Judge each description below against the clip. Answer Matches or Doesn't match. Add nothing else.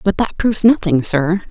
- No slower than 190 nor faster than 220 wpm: Matches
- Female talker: Matches